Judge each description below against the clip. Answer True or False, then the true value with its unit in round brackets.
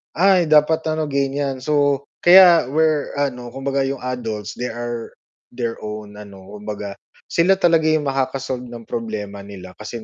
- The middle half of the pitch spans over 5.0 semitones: True (5.6 semitones)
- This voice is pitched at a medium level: False (130 Hz)